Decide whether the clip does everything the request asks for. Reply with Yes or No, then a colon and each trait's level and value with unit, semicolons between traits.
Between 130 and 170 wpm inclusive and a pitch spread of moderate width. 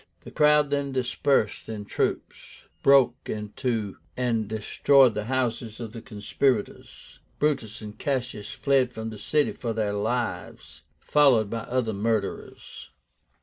Yes: slow, 135 wpm; average, 3.8 semitones